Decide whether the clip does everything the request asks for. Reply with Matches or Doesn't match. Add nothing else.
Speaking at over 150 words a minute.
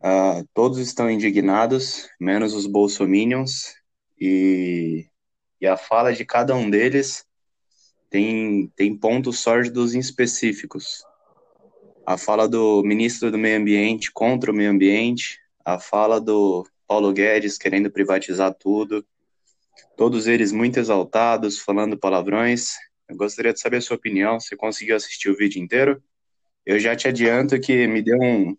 Doesn't match